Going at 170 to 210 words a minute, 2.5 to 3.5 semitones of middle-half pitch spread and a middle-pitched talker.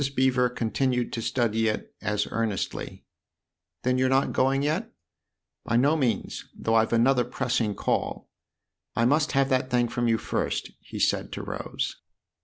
No: average, 175 wpm; average, 2.8 semitones; low, 125 Hz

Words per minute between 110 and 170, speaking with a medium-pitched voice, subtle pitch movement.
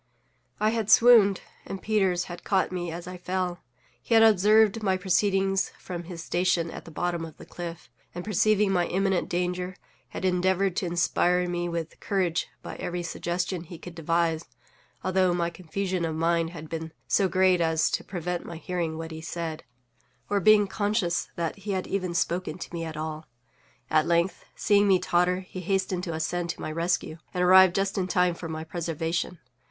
No: average, 185 wpm; medium, 180 Hz; narrow, 2.0 semitones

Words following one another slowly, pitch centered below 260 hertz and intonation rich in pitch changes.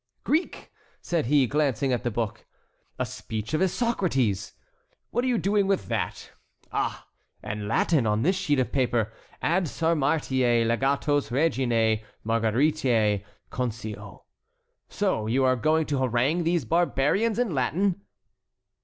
Yes: slow, 130 wpm; low, 135 Hz; wide, 6.3 semitones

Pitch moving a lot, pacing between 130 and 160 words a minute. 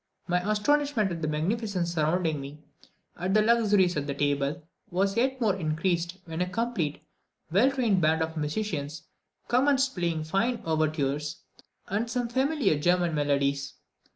Yes: wide, 6.3 semitones; average, 140 wpm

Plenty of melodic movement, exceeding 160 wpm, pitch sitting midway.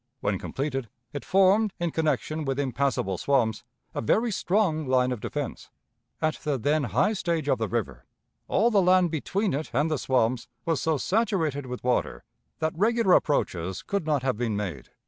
Yes: wide, 5.9 semitones; average, 175 wpm; medium, 145 Hz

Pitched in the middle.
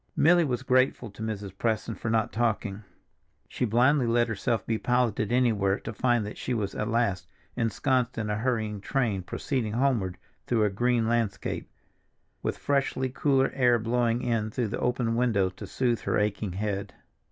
No: low, 115 Hz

